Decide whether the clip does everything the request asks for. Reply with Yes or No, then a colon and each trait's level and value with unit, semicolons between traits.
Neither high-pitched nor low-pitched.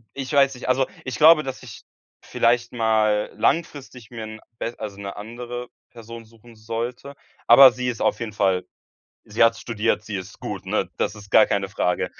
No: low, 115 Hz